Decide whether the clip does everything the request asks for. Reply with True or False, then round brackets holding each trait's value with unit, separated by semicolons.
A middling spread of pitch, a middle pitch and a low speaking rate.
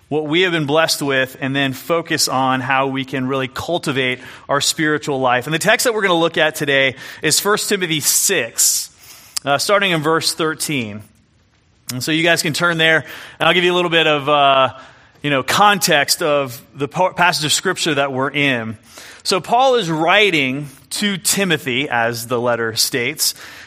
False (4.1 semitones; 145 Hz; 190 wpm)